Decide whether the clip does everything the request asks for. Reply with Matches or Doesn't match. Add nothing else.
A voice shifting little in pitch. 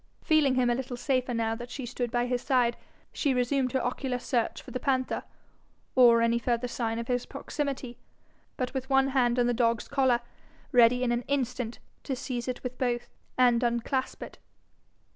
Matches